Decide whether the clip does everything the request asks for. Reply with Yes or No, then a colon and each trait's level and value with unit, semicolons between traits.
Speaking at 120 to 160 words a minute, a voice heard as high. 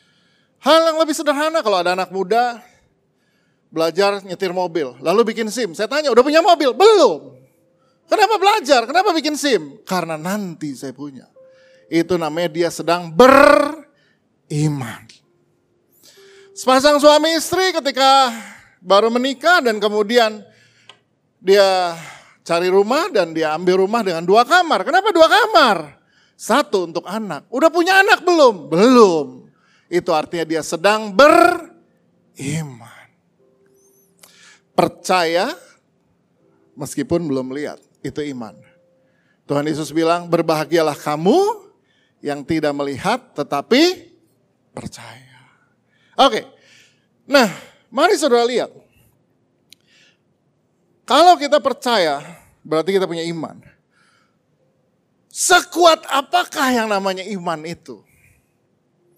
No: average, 105 wpm; high, 200 Hz